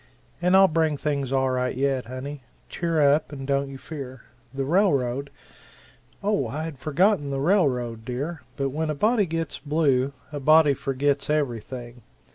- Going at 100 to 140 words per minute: No, average, 165 wpm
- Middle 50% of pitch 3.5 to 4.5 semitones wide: No, average, 3.1 semitones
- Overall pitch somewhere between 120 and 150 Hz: Yes, medium, 140 Hz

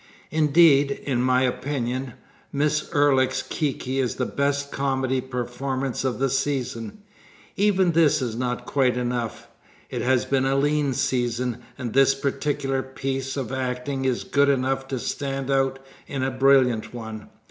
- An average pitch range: No, narrow, 1.8 semitones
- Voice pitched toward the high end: No, low, 135 Hz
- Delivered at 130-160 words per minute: Yes, average, 145 wpm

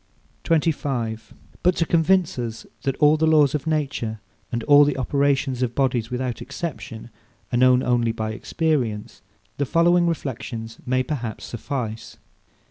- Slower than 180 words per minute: Yes, average, 140 wpm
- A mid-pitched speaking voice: No, low, 130 Hz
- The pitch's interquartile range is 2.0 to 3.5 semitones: No, average, 4.5 semitones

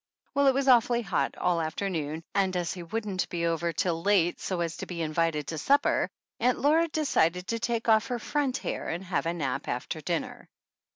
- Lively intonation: Yes, wide, 6.1 semitones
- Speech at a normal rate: No, fast, 210 wpm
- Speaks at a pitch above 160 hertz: Yes, medium, 185 Hz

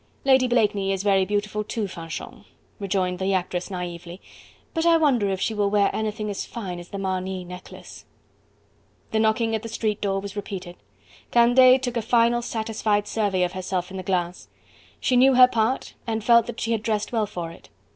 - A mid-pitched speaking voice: No, high, 205 Hz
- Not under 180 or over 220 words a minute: Yes, average, 190 wpm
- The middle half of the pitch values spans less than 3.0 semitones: No, average, 3.6 semitones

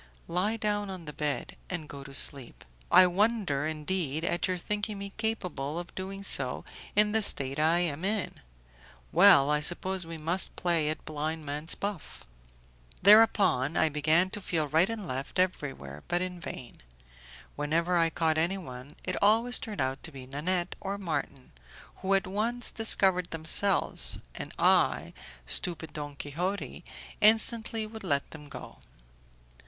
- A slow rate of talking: No, average, 155 wpm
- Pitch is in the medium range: Yes, medium, 175 Hz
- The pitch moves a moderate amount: Yes, average, 4.8 semitones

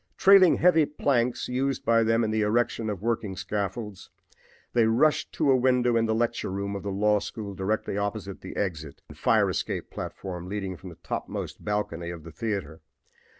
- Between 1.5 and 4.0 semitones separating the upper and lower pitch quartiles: Yes, average, 3.5 semitones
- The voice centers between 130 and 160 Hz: No, low, 105 Hz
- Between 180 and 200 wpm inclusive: Yes, average, 185 wpm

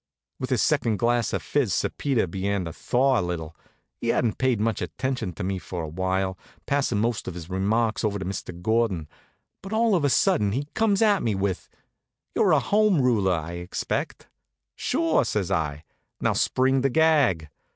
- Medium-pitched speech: No, low, 110 Hz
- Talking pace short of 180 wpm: No, average, 185 wpm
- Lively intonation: Yes, wide, 6.2 semitones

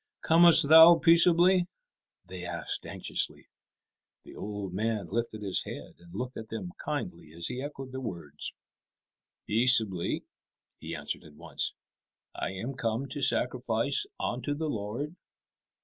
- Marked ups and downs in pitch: Yes, wide, 6.5 semitones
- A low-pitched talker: Yes, low, 115 Hz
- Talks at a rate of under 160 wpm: Yes, slow, 135 wpm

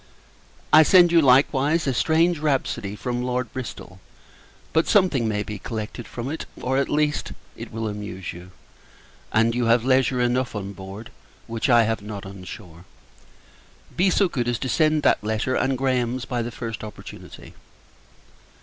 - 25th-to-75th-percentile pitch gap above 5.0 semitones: No, average, 4.0 semitones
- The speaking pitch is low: Yes, low, 120 Hz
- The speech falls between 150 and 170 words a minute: Yes, average, 165 wpm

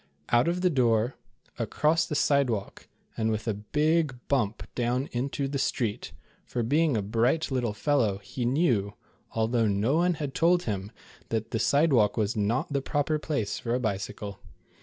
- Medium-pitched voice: No, low, 120 Hz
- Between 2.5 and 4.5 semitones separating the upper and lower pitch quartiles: No, average, 5.1 semitones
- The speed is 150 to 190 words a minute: Yes, average, 165 wpm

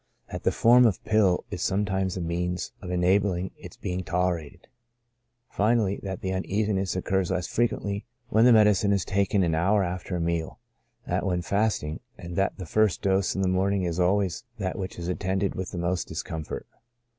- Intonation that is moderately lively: No, narrow, 2.2 semitones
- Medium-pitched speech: No, very low, 95 Hz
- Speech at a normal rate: Yes, average, 185 wpm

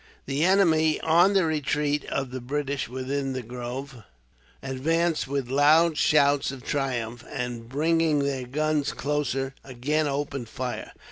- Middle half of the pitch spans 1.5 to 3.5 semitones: Yes, average, 2.9 semitones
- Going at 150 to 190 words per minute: No, slow, 135 wpm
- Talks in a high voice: No, medium, 140 Hz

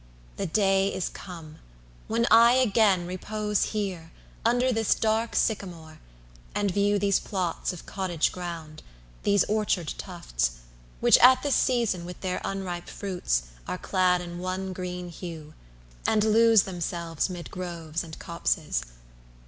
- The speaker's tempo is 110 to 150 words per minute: Yes, average, 140 wpm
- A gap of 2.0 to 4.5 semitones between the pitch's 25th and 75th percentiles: Yes, average, 3.5 semitones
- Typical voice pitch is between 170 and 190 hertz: Yes, medium, 185 Hz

